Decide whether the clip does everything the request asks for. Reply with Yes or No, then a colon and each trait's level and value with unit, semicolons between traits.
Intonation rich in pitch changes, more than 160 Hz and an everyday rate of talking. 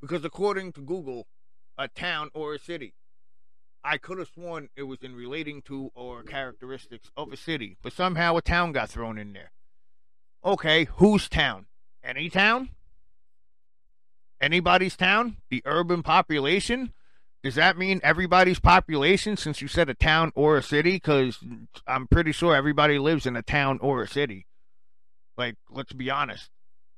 No: wide, 8.9 semitones; medium, 140 Hz; average, 155 wpm